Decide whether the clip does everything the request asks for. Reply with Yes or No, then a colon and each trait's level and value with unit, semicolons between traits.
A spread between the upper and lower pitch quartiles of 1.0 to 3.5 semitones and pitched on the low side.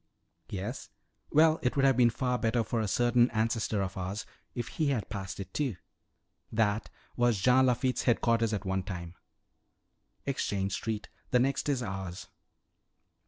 No: average, 4.1 semitones; low, 115 Hz